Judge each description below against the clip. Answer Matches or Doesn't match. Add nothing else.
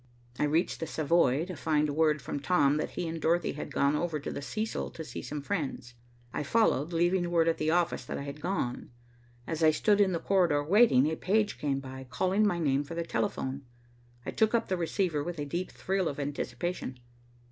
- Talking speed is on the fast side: Matches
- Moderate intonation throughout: Matches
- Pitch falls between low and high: Matches